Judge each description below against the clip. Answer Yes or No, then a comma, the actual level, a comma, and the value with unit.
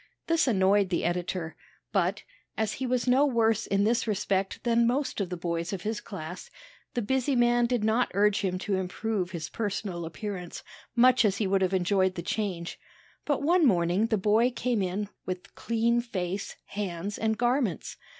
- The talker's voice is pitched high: Yes, high, 205 Hz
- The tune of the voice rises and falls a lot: No, average, 4.2 semitones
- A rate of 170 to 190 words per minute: Yes, average, 180 wpm